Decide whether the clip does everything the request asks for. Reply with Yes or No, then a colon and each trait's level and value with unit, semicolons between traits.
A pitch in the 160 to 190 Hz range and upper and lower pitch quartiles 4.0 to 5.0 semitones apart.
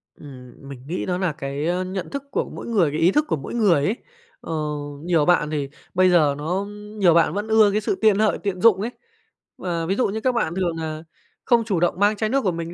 Yes: medium, 185 Hz; average, 4.4 semitones